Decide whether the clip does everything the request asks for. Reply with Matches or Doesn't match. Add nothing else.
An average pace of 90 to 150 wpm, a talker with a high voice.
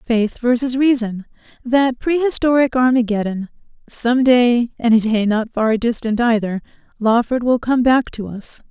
Matches